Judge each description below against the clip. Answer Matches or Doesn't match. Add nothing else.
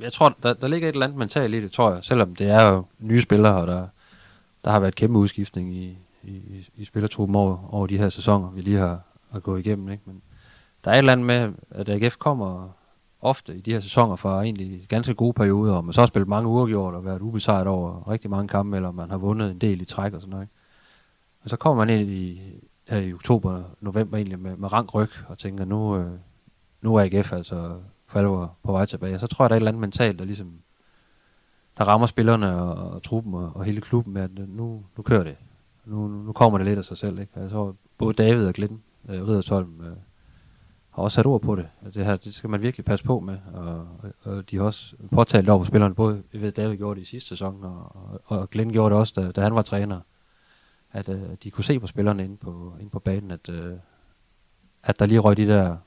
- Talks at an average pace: Doesn't match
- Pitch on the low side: Matches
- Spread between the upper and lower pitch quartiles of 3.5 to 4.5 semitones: Doesn't match